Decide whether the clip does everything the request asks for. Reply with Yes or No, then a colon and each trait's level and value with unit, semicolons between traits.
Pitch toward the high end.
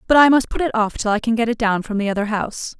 Yes: high, 225 Hz